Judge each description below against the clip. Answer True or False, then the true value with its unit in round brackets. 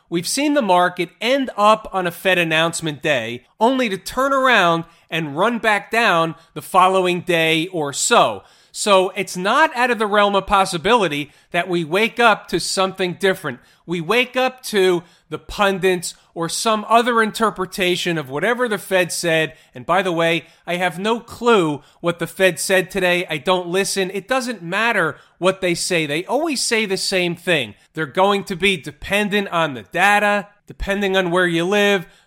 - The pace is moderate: True (180 wpm)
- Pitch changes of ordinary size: True (3.4 semitones)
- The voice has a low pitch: False (185 Hz)